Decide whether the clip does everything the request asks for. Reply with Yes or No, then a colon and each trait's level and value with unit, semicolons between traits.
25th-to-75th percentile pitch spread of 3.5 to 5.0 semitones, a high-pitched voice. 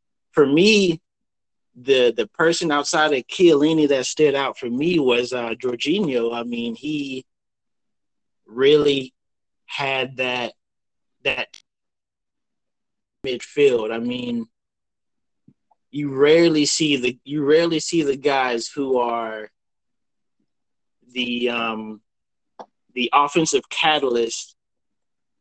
No: average, 4.5 semitones; medium, 140 Hz